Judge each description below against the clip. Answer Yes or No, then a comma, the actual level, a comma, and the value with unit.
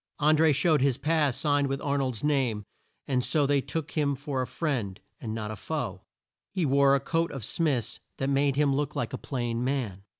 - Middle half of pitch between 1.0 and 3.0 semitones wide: Yes, narrow, 2.6 semitones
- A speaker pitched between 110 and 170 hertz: Yes, medium, 140 Hz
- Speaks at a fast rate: Yes, fast, 210 wpm